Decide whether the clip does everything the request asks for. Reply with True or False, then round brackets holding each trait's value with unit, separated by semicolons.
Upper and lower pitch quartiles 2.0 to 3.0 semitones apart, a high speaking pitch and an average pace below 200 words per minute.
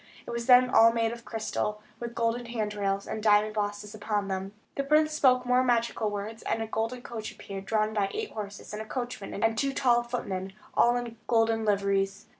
False (2.6 semitones; 225 Hz; 205 wpm)